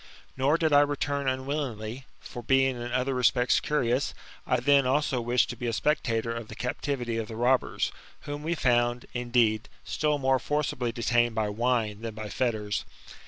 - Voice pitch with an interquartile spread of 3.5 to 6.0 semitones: No, average, 3.0 semitones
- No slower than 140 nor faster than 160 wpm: No, average, 170 wpm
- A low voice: Yes, low, 125 Hz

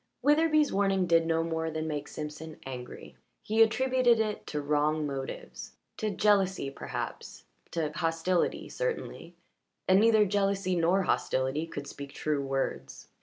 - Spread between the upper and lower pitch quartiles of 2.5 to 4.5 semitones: No, wide, 5.6 semitones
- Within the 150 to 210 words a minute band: No, slow, 135 wpm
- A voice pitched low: No, medium, 165 Hz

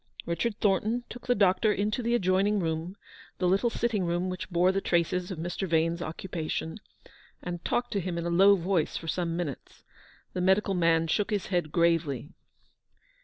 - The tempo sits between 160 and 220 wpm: Yes, average, 175 wpm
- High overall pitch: No, medium, 180 Hz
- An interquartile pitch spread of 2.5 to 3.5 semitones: Yes, average, 3.0 semitones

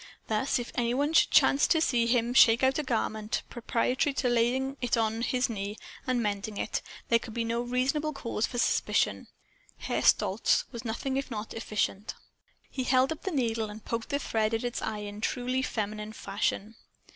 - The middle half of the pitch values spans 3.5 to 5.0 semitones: No, average, 2.9 semitones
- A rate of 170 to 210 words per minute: Yes, average, 190 wpm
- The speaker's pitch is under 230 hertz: No, high, 235 Hz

